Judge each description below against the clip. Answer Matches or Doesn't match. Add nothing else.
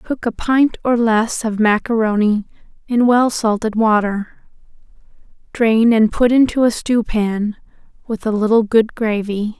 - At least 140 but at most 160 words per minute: Matches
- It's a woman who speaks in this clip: Matches